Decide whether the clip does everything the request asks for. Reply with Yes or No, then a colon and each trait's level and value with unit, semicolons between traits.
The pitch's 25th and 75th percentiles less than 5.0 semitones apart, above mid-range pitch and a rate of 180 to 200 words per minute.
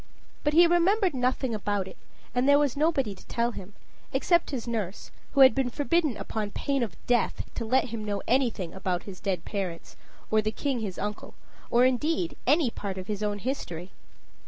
No: average, 5.3 semitones; high, 235 Hz; average, 190 wpm